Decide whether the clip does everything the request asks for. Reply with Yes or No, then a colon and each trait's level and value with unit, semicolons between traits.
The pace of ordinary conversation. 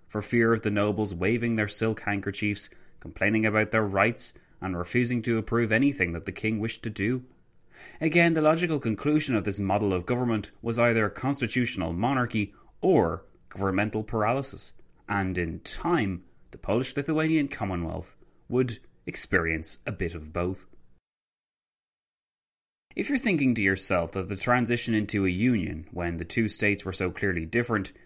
Yes: average, 155 wpm